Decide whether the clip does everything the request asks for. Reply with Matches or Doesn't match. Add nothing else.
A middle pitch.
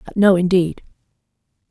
Matches